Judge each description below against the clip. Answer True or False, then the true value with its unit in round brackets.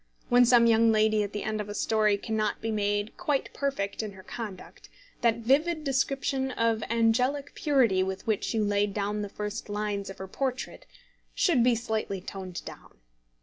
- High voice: True (220 Hz)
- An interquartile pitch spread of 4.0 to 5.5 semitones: False (3.3 semitones)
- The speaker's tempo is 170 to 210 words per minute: True (175 wpm)